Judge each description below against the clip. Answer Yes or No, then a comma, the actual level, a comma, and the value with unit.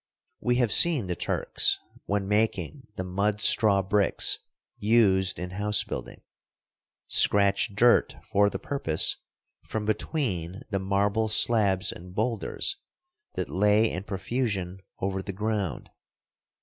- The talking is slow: Yes, slow, 125 wpm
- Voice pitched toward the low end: Yes, low, 100 Hz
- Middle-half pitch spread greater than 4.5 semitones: No, narrow, 2.5 semitones